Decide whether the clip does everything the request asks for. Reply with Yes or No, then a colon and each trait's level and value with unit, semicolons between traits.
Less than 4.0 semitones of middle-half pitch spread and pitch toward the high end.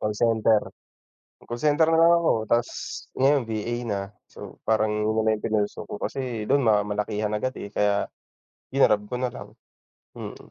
No: average, 3.4 semitones; low, 110 Hz